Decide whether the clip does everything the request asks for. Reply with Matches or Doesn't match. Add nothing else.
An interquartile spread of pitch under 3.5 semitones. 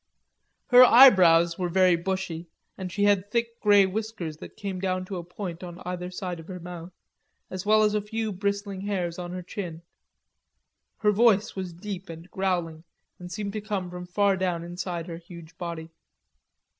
Matches